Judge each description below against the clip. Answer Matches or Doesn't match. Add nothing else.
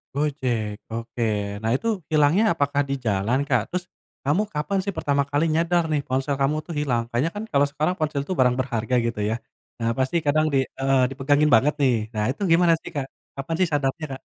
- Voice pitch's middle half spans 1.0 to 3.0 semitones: Doesn't match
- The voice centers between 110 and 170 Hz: Matches